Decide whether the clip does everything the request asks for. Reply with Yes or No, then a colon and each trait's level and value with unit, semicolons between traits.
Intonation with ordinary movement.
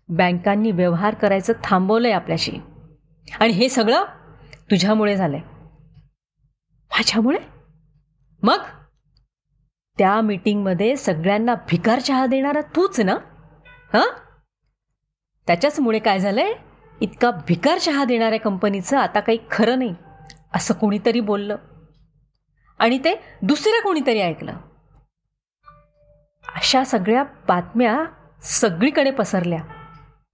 No: wide, 7.3 semitones